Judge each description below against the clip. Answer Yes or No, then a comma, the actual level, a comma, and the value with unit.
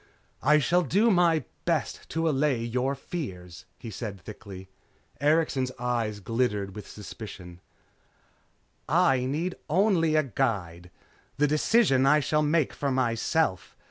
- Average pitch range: No, wide, 6.7 semitones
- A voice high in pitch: No, low, 130 Hz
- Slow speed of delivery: Yes, slow, 125 wpm